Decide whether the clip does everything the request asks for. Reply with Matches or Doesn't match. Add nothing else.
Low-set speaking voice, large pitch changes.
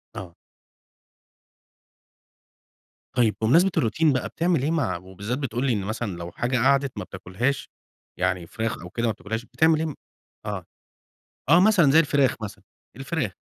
Matches